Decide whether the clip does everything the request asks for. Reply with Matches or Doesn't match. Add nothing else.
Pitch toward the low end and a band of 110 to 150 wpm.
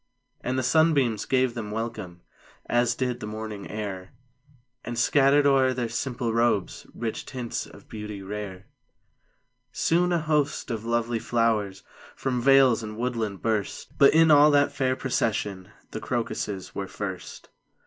Matches